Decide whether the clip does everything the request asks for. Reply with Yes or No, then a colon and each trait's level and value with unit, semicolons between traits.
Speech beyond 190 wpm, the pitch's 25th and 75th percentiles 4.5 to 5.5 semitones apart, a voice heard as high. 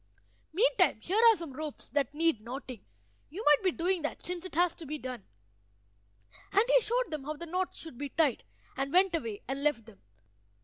Yes: average, 200 wpm; average, 4.9 semitones; very high, 310 Hz